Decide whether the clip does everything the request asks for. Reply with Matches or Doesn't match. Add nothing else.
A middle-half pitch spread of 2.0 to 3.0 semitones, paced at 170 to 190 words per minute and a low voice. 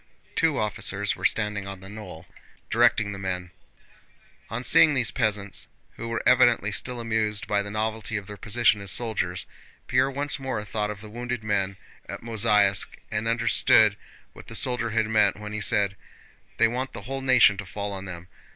Matches